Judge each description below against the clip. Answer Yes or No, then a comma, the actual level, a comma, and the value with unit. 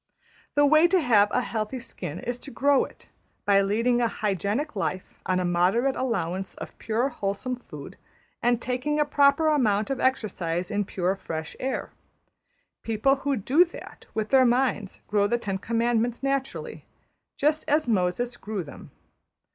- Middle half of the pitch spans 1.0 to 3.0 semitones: No, average, 5.1 semitones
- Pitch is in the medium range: No, high, 235 Hz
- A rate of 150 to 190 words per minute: Yes, average, 160 wpm